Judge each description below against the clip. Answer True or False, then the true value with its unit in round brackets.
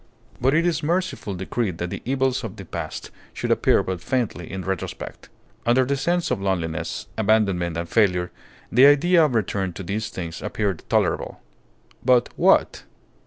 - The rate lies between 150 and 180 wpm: True (165 wpm)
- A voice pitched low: True (110 Hz)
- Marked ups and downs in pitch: True (6.4 semitones)